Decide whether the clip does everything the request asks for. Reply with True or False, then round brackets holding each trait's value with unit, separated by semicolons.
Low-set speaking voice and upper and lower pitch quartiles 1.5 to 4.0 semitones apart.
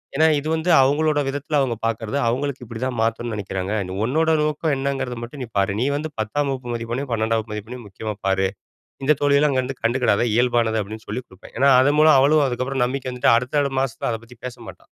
True (125 Hz; 3.7 semitones)